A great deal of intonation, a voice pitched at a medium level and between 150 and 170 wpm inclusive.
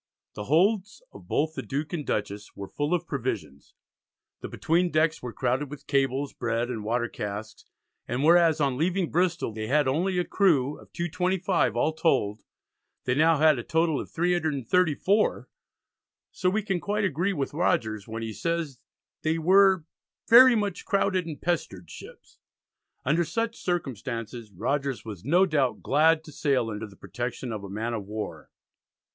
Yes: wide, 6.7 semitones; medium, 150 Hz; average, 165 wpm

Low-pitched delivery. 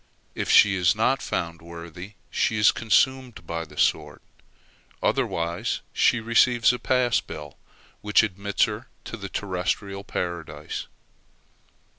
Yes: low, 100 Hz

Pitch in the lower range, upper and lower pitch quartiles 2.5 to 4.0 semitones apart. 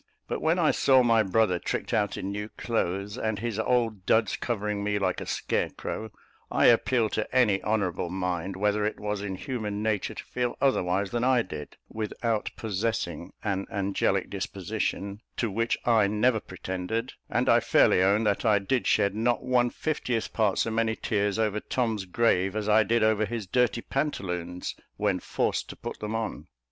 Yes: low, 105 Hz; average, 2.8 semitones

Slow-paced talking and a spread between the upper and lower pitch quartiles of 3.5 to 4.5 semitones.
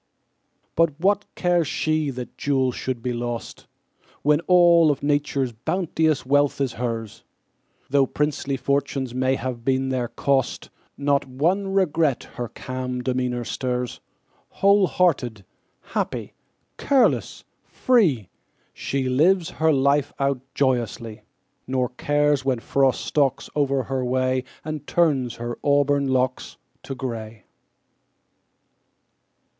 No: slow, 120 wpm; average, 2.8 semitones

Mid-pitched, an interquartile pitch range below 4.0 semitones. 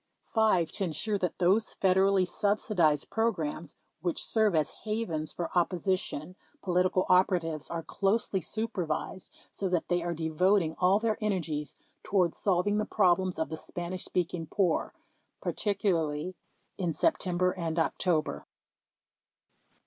Yes: medium, 180 Hz; average, 3.2 semitones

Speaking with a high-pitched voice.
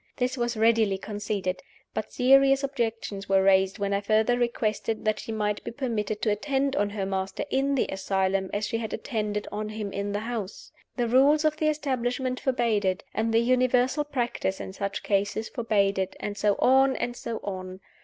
Yes: high, 220 Hz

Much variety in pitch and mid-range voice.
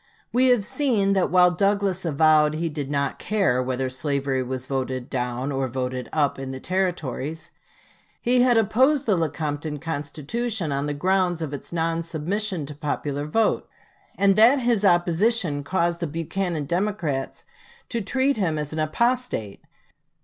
Yes: wide, 5.8 semitones; medium, 165 Hz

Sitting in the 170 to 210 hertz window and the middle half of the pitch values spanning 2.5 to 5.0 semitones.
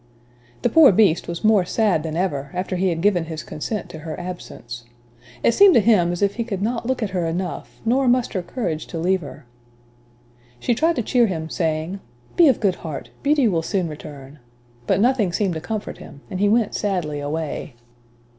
No: medium, 185 Hz; wide, 5.6 semitones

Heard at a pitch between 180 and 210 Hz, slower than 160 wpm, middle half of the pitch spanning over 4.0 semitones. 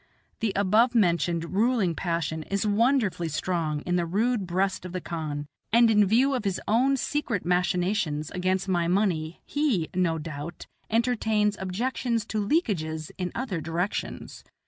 Yes: high, 190 Hz; average, 145 wpm; average, 4.7 semitones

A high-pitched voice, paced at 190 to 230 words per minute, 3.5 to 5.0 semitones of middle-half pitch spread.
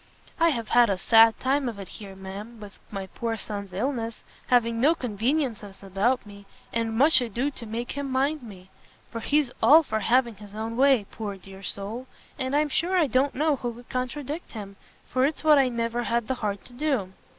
Yes: high, 235 Hz; fast, 205 wpm; average, 4.4 semitones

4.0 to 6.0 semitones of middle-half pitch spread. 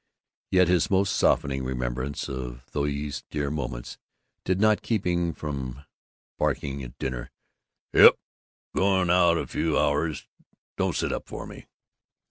Yes: average, 5.2 semitones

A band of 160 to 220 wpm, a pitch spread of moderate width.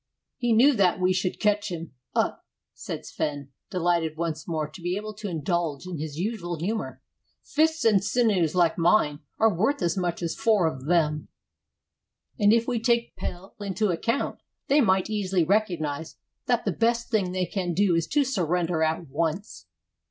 Yes: average, 175 wpm; average, 4.6 semitones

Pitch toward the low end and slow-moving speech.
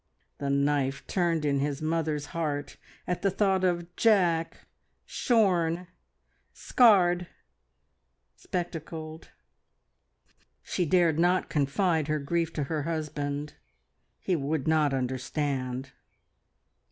No: medium, 160 Hz; slow, 100 wpm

